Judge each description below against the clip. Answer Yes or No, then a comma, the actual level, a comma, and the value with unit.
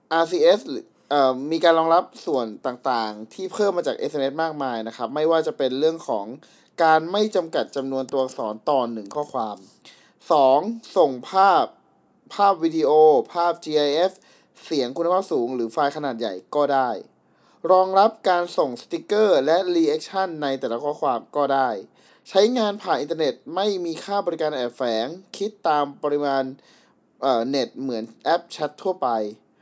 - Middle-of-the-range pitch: Yes, medium, 160 Hz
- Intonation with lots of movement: Yes, wide, 6.1 semitones